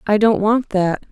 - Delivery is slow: No, fast, 215 wpm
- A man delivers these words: No, female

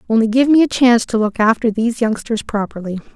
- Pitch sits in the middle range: No, high, 225 Hz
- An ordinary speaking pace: No, fast, 210 wpm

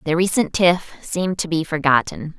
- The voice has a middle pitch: Yes, medium, 170 Hz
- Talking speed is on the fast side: No, average, 175 wpm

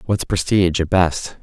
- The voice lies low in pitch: Yes, very low, 90 Hz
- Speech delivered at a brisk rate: No, average, 170 wpm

